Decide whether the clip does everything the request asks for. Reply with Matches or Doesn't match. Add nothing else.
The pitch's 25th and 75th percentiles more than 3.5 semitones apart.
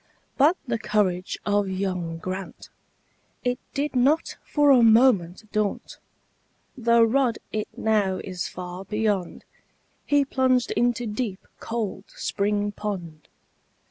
Matches